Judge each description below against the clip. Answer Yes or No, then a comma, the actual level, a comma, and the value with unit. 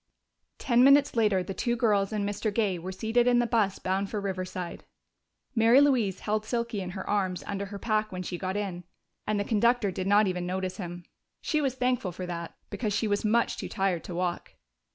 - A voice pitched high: Yes, high, 205 Hz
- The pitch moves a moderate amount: Yes, average, 3.6 semitones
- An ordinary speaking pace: No, fast, 210 wpm